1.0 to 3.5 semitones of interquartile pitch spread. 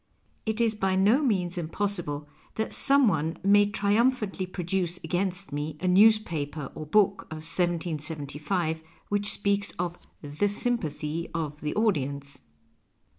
No: average, 4.7 semitones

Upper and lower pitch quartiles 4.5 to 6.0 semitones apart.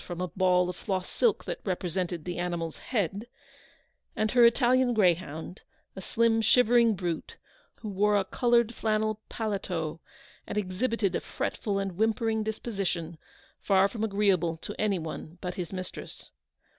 No: average, 3.7 semitones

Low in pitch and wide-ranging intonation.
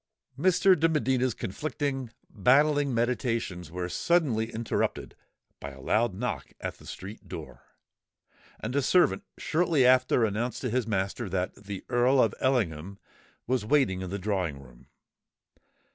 Yes: low, 120 Hz; wide, 5.7 semitones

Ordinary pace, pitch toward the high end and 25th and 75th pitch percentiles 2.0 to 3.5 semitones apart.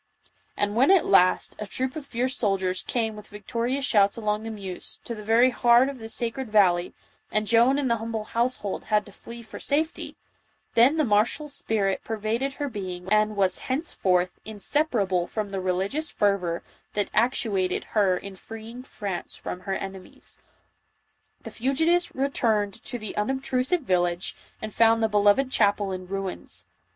No: average, 165 wpm; high, 215 Hz; average, 4.2 semitones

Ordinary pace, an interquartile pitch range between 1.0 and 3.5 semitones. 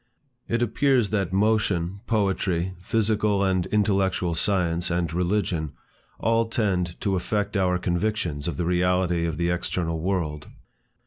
No: slow, 130 wpm; average, 3.1 semitones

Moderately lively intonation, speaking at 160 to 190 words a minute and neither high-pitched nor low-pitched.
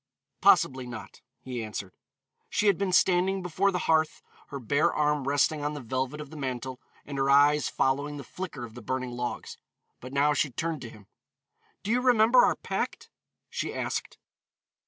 Yes: average, 4.4 semitones; average, 175 wpm; medium, 145 Hz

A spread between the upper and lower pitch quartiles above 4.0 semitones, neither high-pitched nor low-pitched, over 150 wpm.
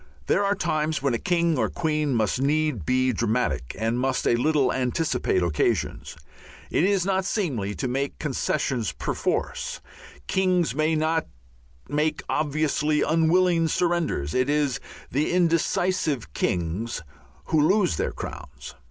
No: average, 4.9 semitones; medium, 150 Hz; slow, 135 wpm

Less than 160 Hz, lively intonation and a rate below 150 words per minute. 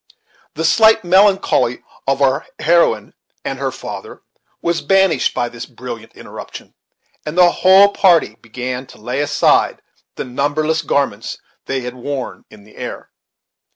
Yes: medium, 140 Hz; wide, 5.7 semitones; average, 140 wpm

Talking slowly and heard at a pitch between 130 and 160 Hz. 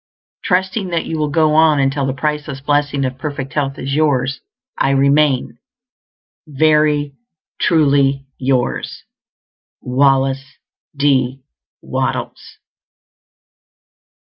Yes: slow, 95 wpm; medium, 140 Hz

